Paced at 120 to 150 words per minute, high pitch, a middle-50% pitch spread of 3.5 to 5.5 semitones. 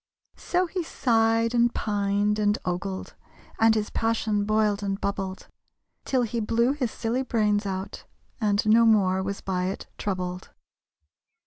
No: average, 140 wpm; high, 210 Hz; narrow, 2.4 semitones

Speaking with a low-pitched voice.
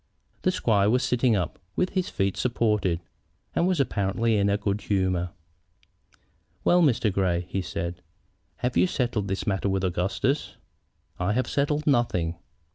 Yes: low, 105 Hz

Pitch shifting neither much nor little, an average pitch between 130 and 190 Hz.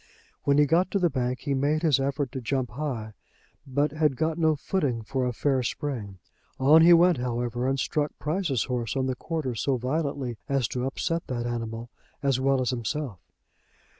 Yes: average, 3.5 semitones; low, 135 Hz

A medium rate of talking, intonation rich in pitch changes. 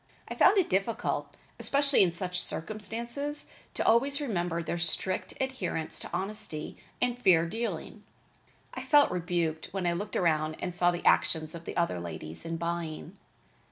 Yes: average, 160 wpm; wide, 5.7 semitones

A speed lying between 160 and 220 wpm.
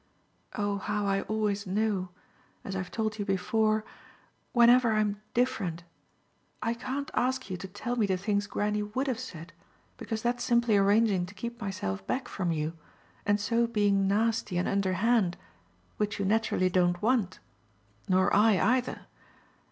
No: average, 150 wpm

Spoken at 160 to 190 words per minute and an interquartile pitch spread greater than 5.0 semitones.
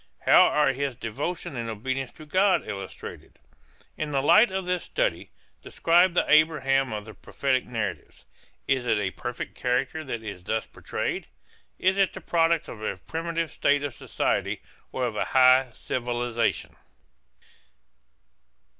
No: average, 145 wpm; wide, 5.6 semitones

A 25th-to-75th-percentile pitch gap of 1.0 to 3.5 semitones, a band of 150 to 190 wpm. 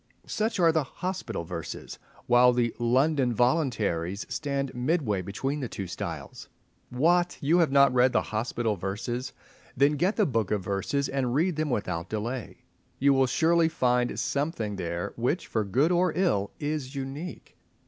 No: wide, 5.5 semitones; average, 160 wpm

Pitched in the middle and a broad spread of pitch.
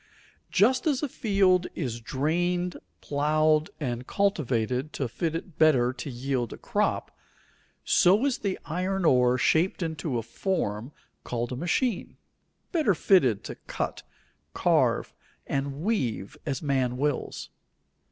Yes: medium, 155 Hz; wide, 6.4 semitones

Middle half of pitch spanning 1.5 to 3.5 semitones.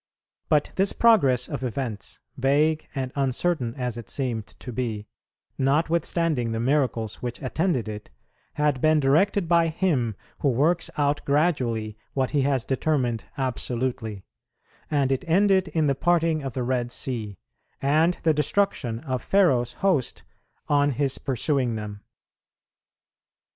No: average, 4.5 semitones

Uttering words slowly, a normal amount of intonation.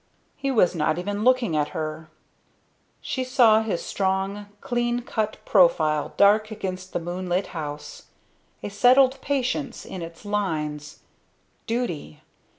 No: slow, 125 wpm; wide, 6.3 semitones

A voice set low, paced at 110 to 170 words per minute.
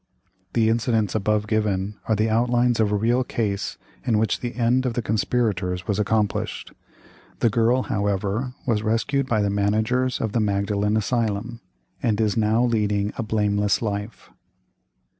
Yes: low, 110 Hz; average, 155 wpm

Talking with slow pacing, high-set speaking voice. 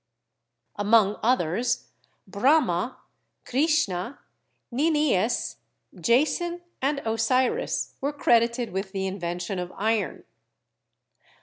Yes: slow, 85 wpm; high, 230 Hz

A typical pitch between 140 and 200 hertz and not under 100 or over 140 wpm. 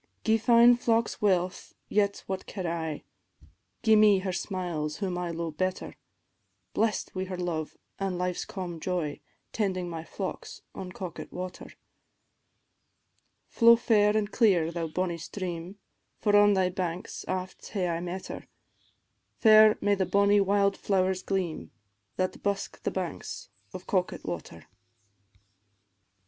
Yes: medium, 185 Hz; slow, 135 wpm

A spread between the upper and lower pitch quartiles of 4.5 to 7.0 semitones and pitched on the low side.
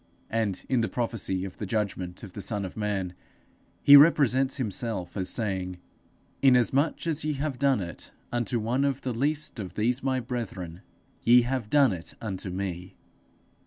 Yes: wide, 5.6 semitones; low, 115 Hz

